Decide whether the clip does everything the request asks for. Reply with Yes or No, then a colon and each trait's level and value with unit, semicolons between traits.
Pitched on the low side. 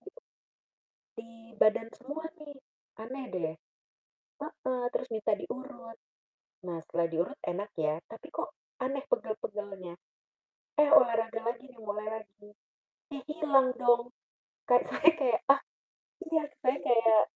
No: high, 235 Hz